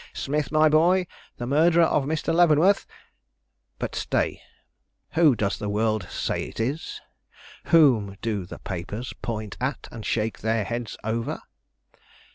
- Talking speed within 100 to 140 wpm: Yes, slow, 135 wpm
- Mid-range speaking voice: No, low, 120 Hz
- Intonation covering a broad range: Yes, wide, 6.3 semitones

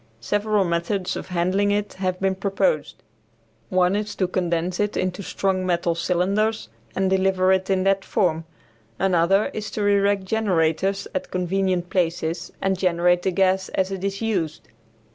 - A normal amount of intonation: No, narrow, 1.8 semitones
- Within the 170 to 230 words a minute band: No, average, 155 wpm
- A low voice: No, high, 190 Hz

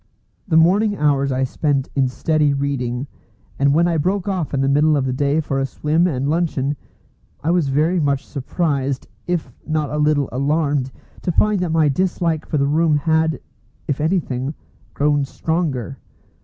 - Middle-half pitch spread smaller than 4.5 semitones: Yes, average, 2.9 semitones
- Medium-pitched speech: Yes, medium, 150 Hz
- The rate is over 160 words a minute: Yes, average, 170 wpm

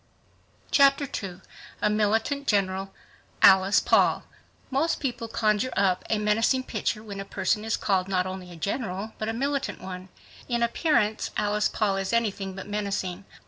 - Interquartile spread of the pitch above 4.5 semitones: No, average, 3.3 semitones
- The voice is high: Yes, high, 210 Hz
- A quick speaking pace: No, average, 150 wpm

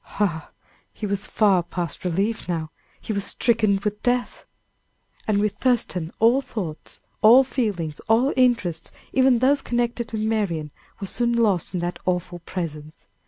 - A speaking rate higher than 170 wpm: No, average, 150 wpm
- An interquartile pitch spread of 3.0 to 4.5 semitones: No, average, 5.1 semitones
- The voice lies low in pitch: No, high, 210 Hz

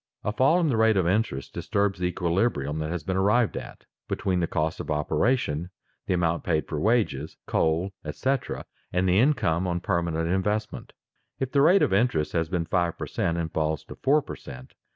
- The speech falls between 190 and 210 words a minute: Yes, average, 195 wpm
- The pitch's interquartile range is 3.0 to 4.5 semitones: No, average, 5.3 semitones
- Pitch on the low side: Yes, very low, 90 Hz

